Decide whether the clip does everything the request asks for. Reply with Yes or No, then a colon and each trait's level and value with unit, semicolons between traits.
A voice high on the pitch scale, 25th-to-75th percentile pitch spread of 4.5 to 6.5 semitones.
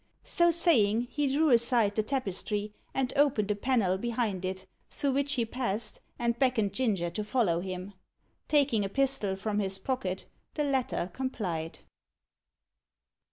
Yes: high, 225 Hz; average, 5.3 semitones